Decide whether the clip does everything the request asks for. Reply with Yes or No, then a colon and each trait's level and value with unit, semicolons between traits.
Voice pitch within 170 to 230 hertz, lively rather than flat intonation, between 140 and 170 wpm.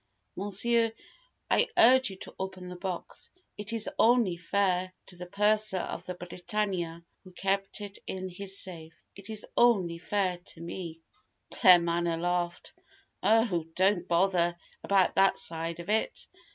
No: medium, 185 Hz; average, 2.8 semitones; average, 150 wpm